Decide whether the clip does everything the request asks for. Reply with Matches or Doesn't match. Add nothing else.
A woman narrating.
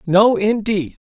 Doesn't match